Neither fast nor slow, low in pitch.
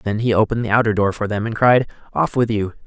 No: fast, 270 wpm; low, 110 Hz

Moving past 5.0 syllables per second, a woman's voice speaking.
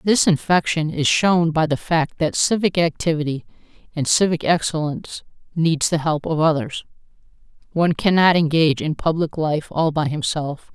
No: 4.9 syllables/s; female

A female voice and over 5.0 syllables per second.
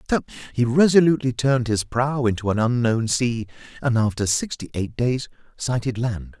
No: male; 5.2 syllables/s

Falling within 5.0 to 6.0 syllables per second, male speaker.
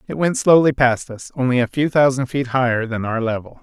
Yes: 5.5 syllables/s; male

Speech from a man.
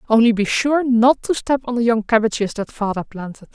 No: female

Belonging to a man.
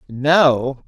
No: female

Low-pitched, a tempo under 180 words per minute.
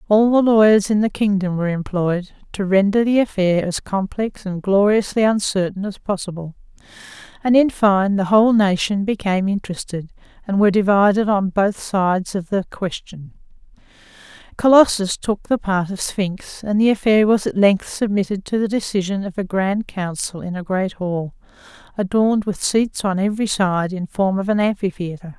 No: high, 200 Hz; average, 170 wpm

